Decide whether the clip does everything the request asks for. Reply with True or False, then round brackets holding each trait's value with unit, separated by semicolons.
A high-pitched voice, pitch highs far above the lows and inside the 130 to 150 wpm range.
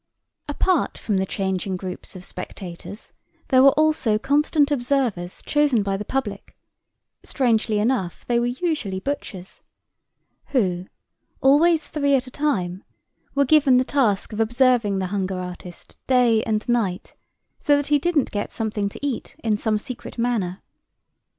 True (230 Hz; 6.1 semitones; 140 wpm)